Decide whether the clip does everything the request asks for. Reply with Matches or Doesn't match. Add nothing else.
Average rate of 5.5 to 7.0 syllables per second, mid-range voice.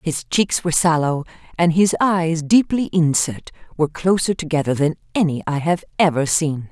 Doesn't match